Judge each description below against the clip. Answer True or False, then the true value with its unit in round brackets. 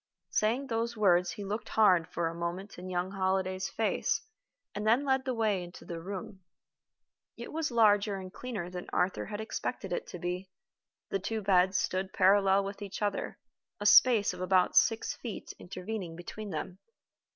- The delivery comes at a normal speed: True (175 wpm)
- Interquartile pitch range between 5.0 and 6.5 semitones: False (3.0 semitones)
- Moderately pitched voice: False (195 Hz)